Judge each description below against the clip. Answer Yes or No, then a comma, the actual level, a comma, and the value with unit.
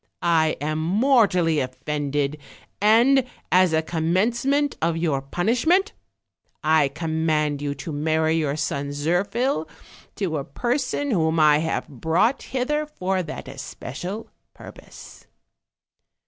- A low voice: No, medium, 160 Hz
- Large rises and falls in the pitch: Yes, wide, 6.4 semitones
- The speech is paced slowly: Yes, slow, 120 wpm